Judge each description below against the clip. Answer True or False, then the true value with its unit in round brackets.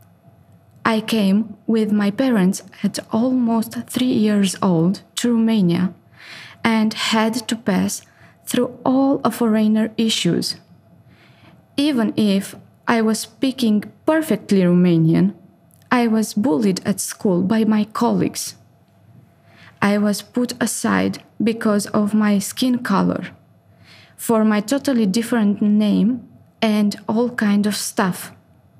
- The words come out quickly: False (115 wpm)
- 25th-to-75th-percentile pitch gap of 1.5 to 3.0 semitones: True (2.7 semitones)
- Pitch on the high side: True (220 Hz)